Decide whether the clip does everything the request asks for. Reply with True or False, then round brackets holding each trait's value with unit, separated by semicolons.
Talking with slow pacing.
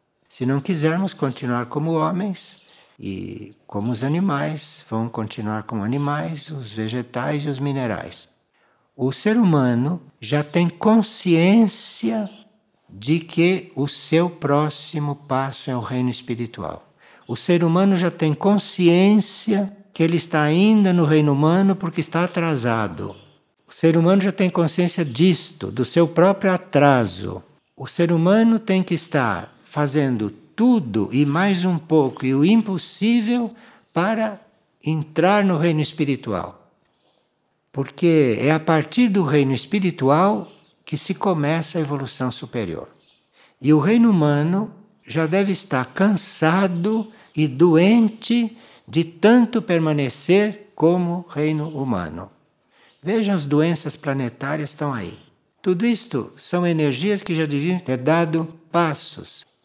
False (130 wpm)